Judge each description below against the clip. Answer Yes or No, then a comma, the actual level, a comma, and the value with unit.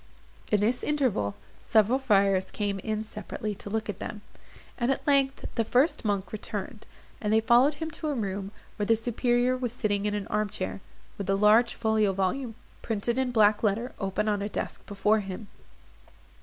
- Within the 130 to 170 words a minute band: No, average, 185 wpm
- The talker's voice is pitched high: Yes, high, 215 Hz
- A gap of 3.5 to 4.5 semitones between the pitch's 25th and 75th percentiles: No, average, 3.1 semitones